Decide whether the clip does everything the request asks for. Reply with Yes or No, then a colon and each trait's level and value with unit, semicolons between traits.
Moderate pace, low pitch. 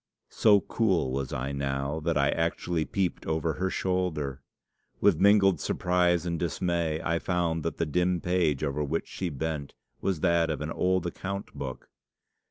Yes: average, 165 wpm; very low, 85 Hz